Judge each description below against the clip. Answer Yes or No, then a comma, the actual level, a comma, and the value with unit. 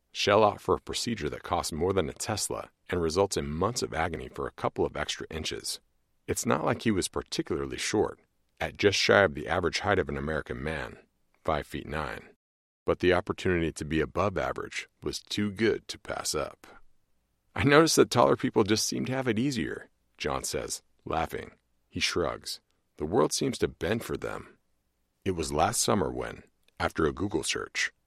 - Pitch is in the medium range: No, low, 100 Hz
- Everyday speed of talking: Yes, average, 190 wpm